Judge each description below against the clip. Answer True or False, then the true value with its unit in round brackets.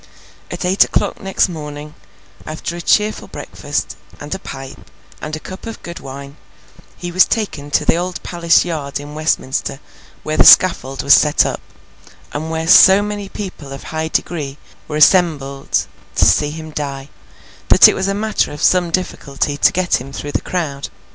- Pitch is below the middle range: False (155 Hz)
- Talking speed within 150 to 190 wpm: True (175 wpm)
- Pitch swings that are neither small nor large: True (4.2 semitones)